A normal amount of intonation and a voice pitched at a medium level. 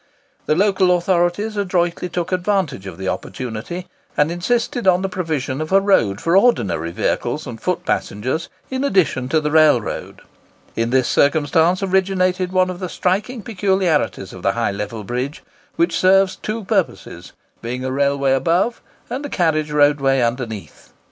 No: wide, 6.1 semitones; medium, 170 Hz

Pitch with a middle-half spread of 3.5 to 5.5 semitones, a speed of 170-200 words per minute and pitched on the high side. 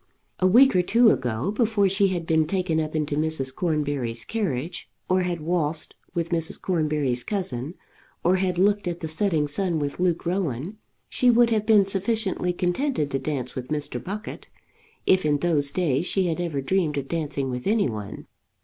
No: average, 4.7 semitones; average, 180 wpm; medium, 170 Hz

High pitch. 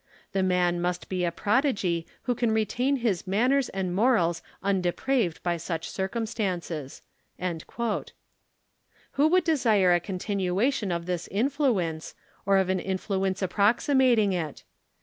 Yes: high, 195 Hz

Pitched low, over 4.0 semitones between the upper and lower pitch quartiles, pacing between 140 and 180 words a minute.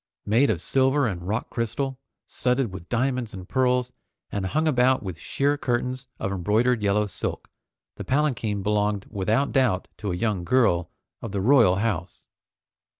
Yes: low, 115 Hz; average, 4.7 semitones; average, 155 wpm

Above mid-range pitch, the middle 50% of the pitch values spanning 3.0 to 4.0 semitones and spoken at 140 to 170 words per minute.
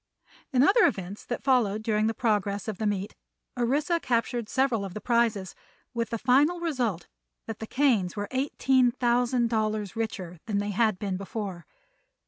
Yes: high, 225 Hz; average, 3.5 semitones; average, 165 wpm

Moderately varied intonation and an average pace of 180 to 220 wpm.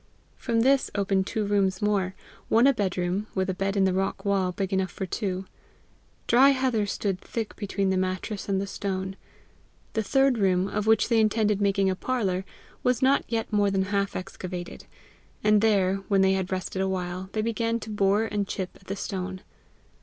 No: narrow, 2.3 semitones; average, 190 wpm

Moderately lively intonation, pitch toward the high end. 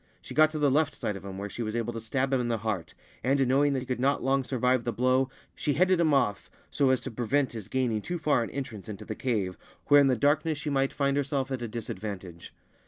No: average, 3.9 semitones; low, 130 Hz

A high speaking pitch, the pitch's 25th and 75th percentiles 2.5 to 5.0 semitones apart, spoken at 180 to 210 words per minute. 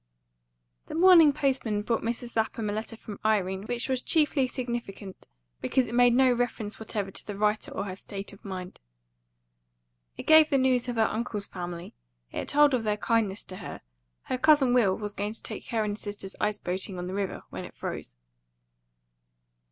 Yes: high, 220 Hz; average, 3.8 semitones; average, 190 wpm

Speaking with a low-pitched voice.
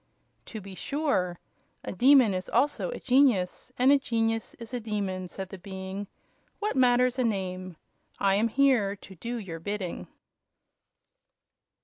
No: high, 215 Hz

